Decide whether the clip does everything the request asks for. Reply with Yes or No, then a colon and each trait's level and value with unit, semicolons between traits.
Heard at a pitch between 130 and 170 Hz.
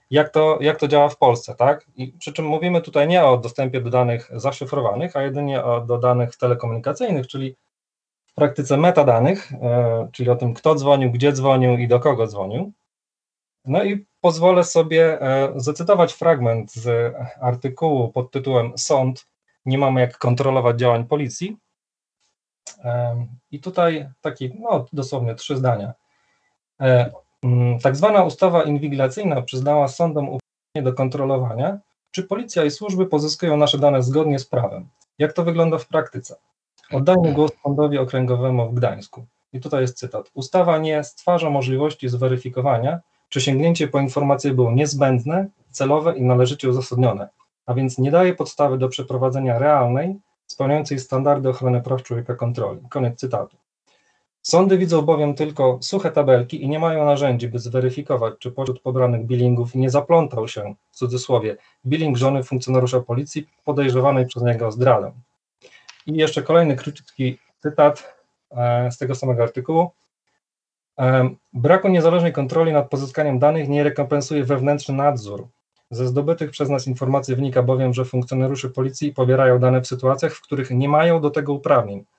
Yes: low, 135 Hz